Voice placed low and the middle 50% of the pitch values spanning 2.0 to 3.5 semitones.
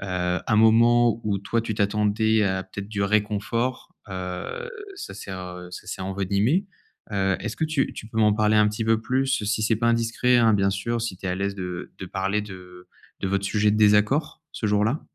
Yes: low, 105 Hz; average, 2.9 semitones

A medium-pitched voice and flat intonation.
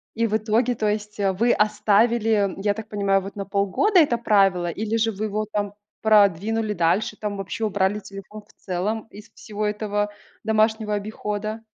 No: high, 210 Hz; narrow, 1.6 semitones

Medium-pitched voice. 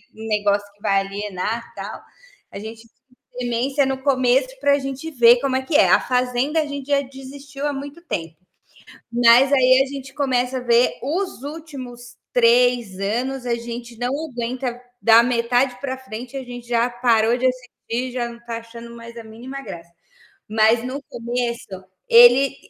No: high, 245 Hz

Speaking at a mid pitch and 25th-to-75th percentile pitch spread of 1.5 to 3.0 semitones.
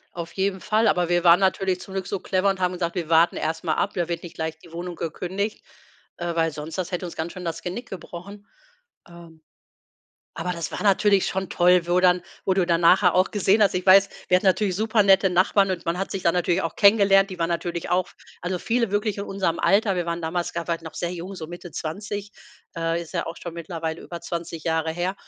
Yes: medium, 180 Hz; narrow, 2.4 semitones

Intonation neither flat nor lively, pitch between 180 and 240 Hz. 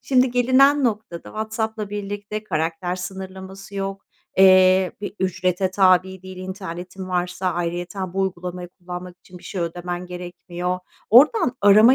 No: narrow, 2.3 semitones; medium, 185 Hz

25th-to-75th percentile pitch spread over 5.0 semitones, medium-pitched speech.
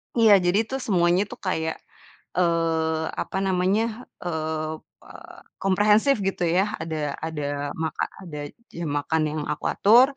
No: average, 4.1 semitones; medium, 175 Hz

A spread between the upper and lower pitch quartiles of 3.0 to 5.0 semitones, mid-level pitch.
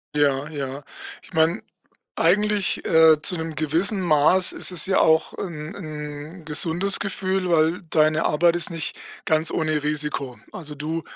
No: narrow, 2.6 semitones; medium, 160 Hz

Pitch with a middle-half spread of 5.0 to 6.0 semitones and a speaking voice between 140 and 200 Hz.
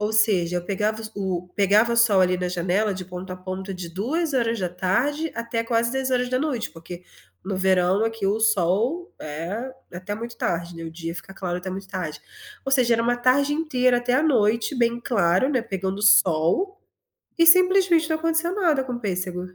No: wide, 5.6 semitones; high, 215 Hz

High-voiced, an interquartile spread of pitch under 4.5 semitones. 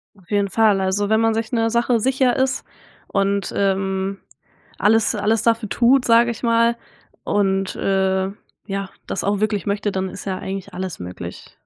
Yes: high, 205 Hz; average, 2.9 semitones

